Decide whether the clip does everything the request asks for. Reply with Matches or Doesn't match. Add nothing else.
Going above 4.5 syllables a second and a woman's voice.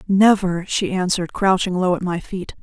Matches